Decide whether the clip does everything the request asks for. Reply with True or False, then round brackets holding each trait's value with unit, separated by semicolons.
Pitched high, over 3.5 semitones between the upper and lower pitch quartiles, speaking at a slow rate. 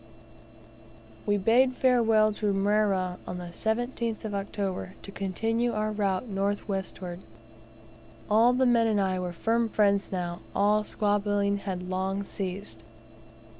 False (205 Hz; 2.5 semitones; 130 wpm)